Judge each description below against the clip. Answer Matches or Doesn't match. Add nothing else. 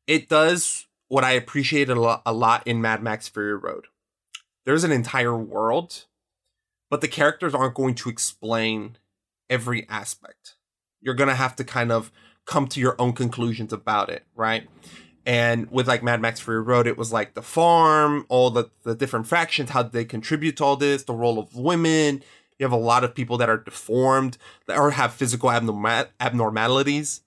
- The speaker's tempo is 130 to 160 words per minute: Doesn't match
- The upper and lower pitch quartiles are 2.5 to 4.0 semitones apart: Matches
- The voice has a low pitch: Matches